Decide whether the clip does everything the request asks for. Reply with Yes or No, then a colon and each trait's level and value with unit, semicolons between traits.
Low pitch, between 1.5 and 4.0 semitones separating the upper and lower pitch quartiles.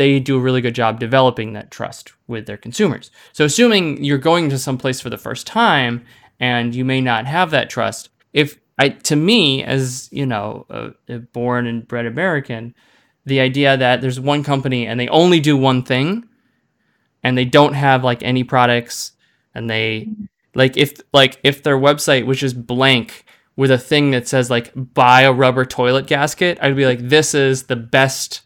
Yes: low, 130 Hz; average, 2.7 semitones